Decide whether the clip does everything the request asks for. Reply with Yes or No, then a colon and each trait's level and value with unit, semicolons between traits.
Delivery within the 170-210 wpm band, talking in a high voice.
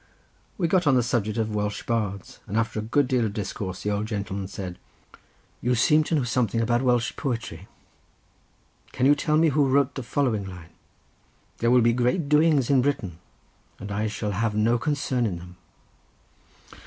No: average, 180 wpm; low, 115 Hz